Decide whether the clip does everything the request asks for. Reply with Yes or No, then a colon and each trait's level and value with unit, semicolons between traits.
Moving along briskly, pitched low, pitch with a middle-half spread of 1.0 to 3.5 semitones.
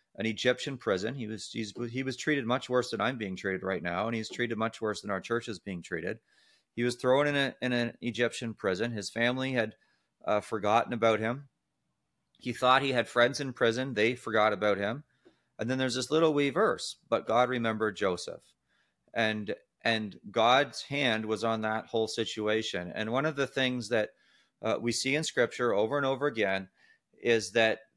No: average, 195 wpm; low, 115 Hz; average, 2.8 semitones